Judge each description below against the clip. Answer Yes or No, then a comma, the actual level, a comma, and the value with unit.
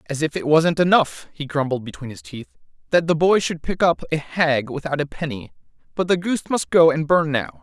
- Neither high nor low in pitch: Yes, medium, 155 Hz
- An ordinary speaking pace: No, fast, 230 wpm